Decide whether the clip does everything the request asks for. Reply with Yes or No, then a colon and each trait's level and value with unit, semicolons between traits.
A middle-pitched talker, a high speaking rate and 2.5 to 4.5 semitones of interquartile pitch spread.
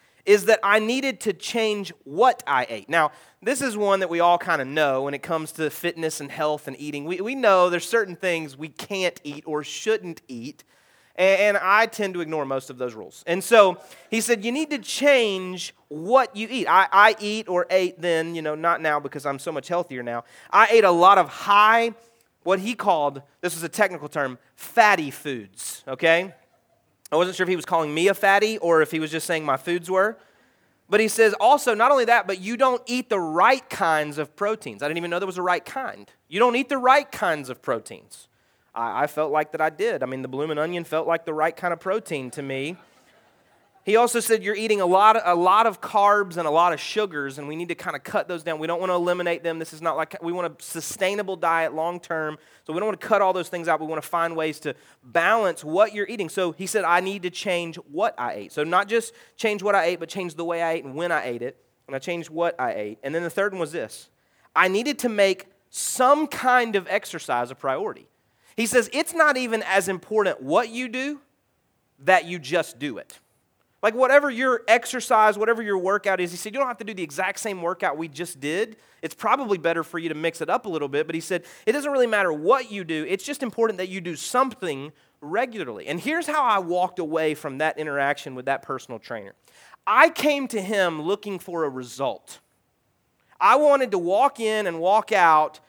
No: medium, 180 Hz; fast, 235 wpm; wide, 5.4 semitones